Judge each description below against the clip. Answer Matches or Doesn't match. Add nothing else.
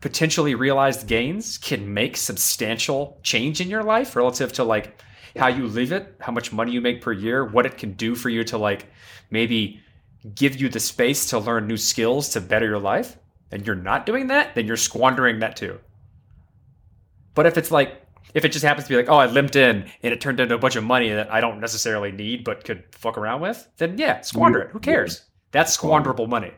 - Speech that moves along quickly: Matches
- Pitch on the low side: Matches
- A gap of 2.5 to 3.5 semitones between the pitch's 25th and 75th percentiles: Doesn't match